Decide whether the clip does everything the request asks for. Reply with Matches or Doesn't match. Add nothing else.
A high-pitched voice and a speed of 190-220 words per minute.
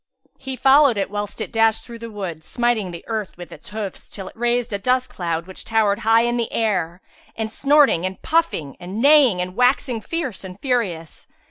Matches